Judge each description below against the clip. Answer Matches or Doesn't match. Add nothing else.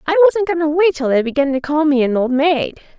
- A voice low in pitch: Doesn't match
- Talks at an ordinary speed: Doesn't match